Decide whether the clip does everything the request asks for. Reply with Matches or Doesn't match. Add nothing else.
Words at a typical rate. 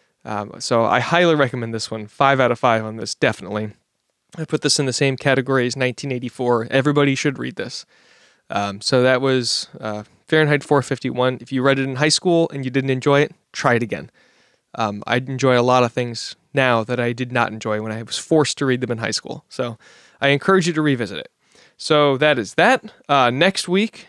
Doesn't match